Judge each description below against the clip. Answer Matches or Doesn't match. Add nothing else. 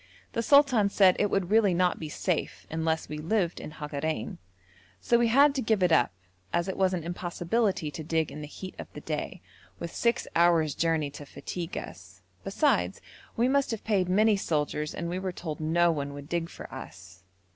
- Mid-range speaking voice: Matches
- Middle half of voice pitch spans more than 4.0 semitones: Matches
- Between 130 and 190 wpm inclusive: Doesn't match